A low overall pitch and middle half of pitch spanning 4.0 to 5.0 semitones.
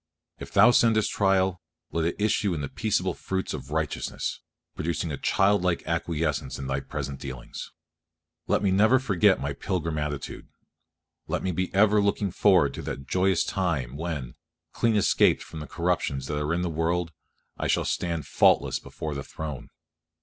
Yes: very low, 85 Hz; average, 4.4 semitones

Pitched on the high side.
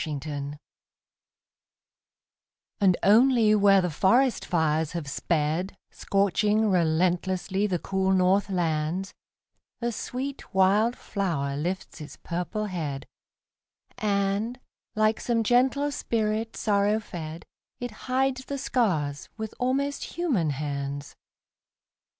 Yes: high, 195 Hz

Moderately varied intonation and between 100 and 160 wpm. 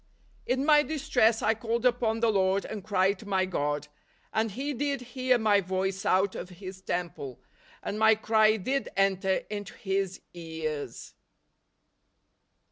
Yes: average, 3.5 semitones; average, 155 wpm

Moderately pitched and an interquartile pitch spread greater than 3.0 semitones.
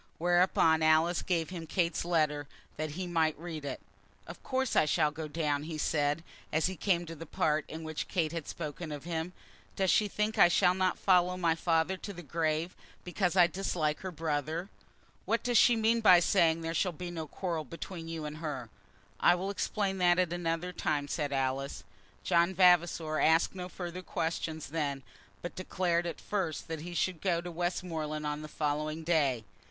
No: medium, 165 Hz; narrow, 2.6 semitones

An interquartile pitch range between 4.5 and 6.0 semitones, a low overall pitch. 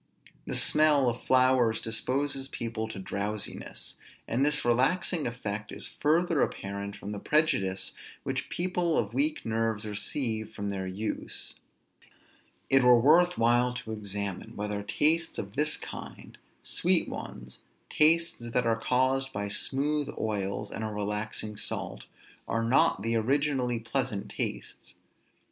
Yes: average, 4.9 semitones; low, 115 Hz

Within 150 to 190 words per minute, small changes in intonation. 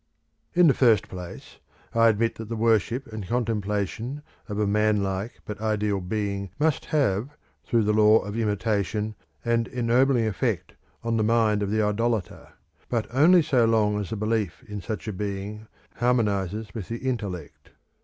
Yes: average, 165 wpm; narrow, 2.2 semitones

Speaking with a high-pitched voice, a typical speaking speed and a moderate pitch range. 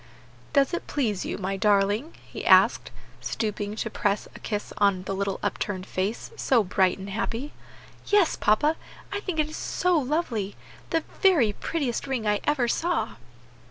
No: high, 225 Hz; average, 160 wpm; wide, 6.9 semitones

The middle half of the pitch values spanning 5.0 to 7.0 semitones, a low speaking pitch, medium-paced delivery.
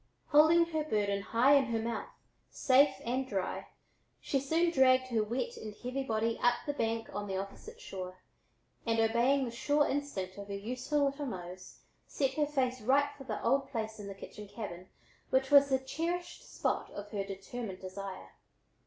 No: wide, 5.4 semitones; high, 245 Hz; average, 180 wpm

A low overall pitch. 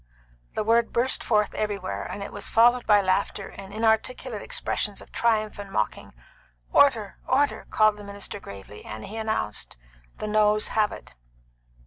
No: high, 210 Hz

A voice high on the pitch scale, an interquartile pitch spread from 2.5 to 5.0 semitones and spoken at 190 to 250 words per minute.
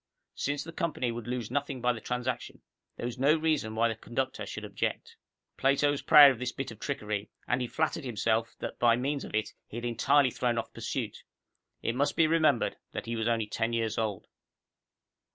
No: low, 120 Hz; average, 3.5 semitones; fast, 205 wpm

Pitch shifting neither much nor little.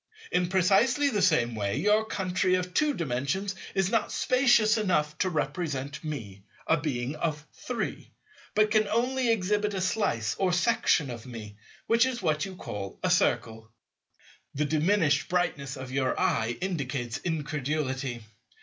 No: wide, 7.6 semitones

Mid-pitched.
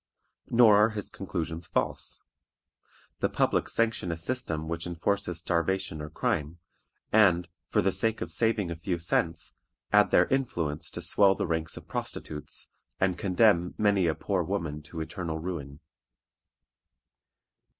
No: very low, 90 Hz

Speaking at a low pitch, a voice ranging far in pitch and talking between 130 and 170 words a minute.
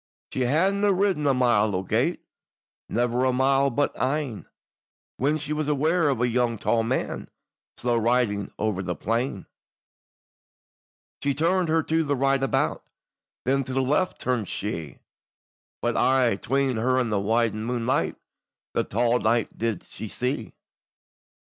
No: low, 125 Hz; average, 3.7 semitones; average, 150 wpm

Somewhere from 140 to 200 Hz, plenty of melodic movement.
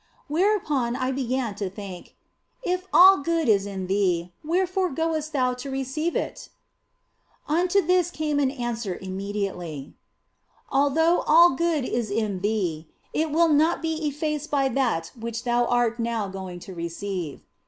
No: very high, 255 Hz; wide, 7.7 semitones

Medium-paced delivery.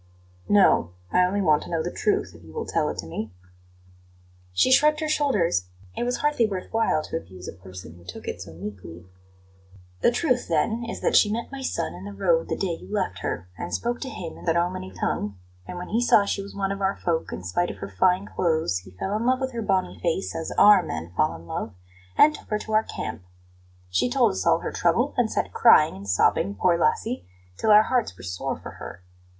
No: fast, 235 wpm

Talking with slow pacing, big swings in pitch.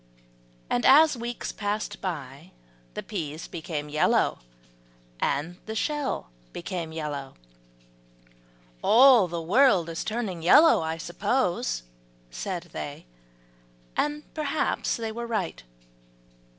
Yes: slow, 105 wpm; wide, 6.8 semitones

